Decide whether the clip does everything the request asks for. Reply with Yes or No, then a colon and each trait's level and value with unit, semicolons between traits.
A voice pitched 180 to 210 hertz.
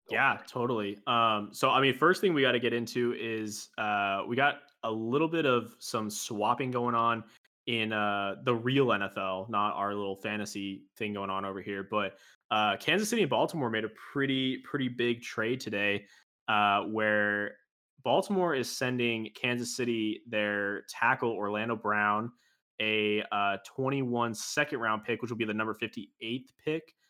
No: low, 115 Hz